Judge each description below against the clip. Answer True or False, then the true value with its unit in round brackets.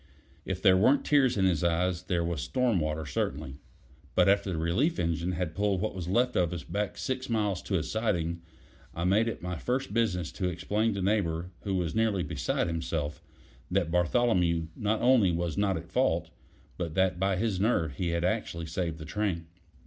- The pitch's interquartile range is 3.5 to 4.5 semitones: True (3.9 semitones)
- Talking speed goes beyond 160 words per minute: True (195 wpm)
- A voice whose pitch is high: False (90 Hz)